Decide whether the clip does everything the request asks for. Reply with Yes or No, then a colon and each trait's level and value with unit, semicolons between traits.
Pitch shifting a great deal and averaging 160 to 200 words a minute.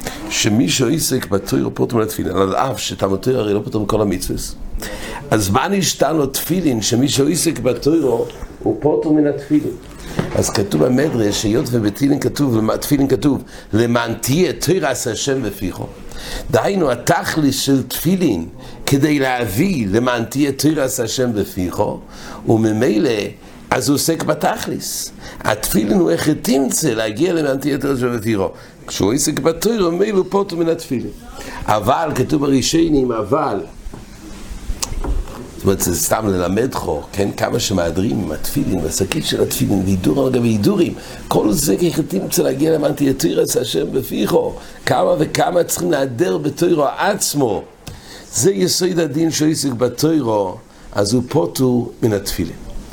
No: wide, 6.2 semitones; slow, 135 wpm